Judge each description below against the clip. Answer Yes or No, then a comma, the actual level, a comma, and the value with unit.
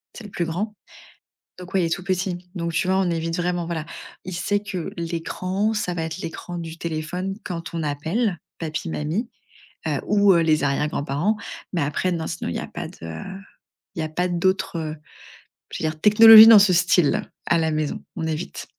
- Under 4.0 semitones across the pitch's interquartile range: Yes, average, 2.9 semitones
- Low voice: No, medium, 170 Hz